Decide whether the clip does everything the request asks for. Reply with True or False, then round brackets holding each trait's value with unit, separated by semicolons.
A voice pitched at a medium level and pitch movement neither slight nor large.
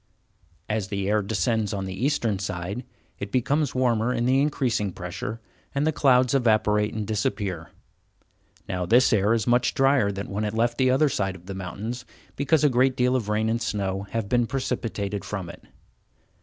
False (110 Hz; 4.1 semitones)